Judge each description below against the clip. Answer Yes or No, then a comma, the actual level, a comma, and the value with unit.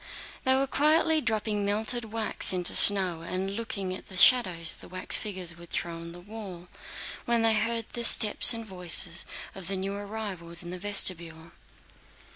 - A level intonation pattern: No, average, 4.1 semitones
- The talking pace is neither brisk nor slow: Yes, average, 165 wpm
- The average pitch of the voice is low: No, high, 195 Hz